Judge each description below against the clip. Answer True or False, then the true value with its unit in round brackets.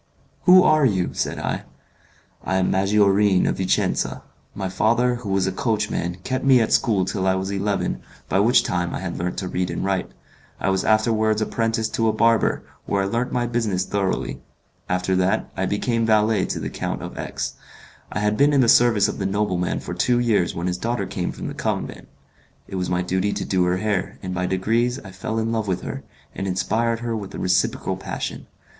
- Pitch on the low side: True (100 Hz)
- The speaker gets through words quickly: True (210 wpm)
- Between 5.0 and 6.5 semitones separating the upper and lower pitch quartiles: False (3.5 semitones)